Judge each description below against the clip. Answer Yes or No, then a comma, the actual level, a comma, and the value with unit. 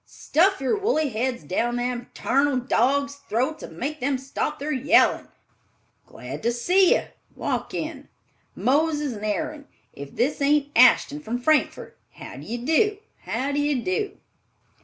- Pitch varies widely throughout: No, average, 3.7 semitones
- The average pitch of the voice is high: Yes, very high, 275 Hz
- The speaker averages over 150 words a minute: No, average, 140 wpm